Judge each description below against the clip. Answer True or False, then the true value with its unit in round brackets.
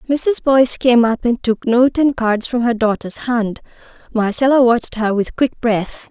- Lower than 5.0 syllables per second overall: True (4.5 syllables/s)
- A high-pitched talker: True (240 Hz)